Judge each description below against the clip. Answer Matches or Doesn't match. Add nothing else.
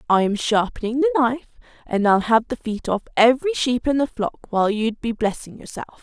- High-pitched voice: Matches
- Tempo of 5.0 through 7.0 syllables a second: Matches